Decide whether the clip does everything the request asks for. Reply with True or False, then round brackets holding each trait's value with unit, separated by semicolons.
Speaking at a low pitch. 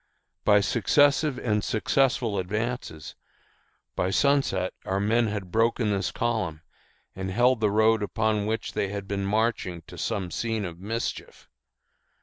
True (105 Hz)